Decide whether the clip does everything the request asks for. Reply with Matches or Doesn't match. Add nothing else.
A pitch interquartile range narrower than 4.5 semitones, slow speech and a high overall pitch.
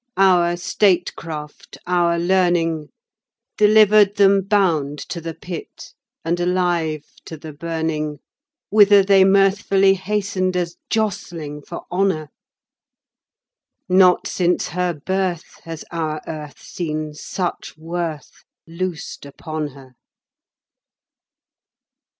Doesn't match